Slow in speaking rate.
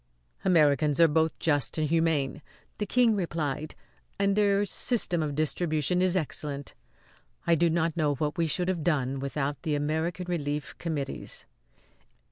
No: average, 145 wpm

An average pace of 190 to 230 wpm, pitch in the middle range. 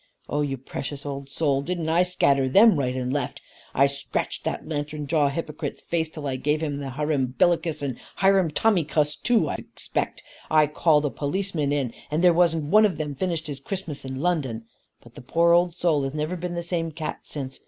Yes: average, 195 wpm; medium, 150 Hz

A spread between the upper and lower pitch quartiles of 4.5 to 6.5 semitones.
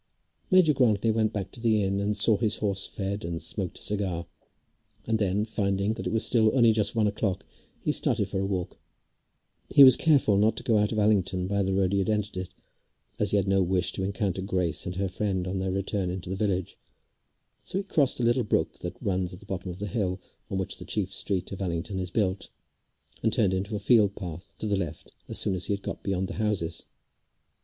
No: narrow, 2.4 semitones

